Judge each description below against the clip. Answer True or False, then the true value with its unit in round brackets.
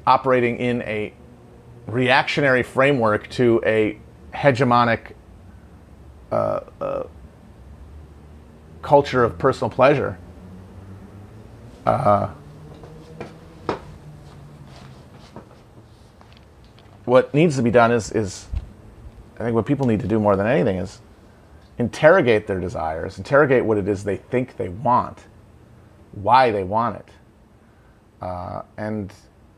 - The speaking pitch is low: True (105 Hz)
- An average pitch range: True (3.7 semitones)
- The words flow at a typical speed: False (100 wpm)